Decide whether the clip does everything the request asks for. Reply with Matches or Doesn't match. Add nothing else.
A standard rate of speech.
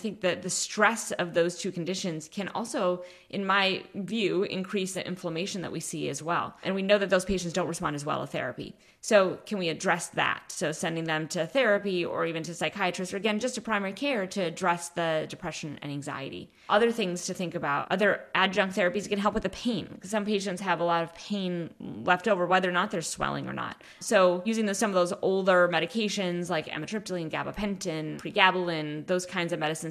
Doesn't match